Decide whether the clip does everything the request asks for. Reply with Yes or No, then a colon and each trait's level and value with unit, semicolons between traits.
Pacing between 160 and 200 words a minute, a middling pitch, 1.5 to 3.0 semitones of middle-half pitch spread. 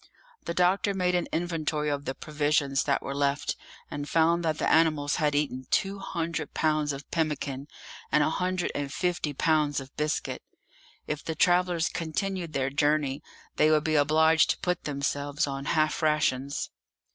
Yes: average, 165 wpm; medium, 155 Hz; narrow, 2.5 semitones